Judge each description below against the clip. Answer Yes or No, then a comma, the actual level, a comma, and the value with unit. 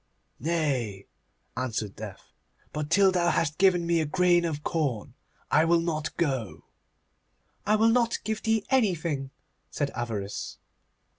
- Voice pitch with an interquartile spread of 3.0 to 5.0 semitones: No, wide, 5.4 semitones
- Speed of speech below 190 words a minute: Yes, slow, 135 wpm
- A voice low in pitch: No, medium, 160 Hz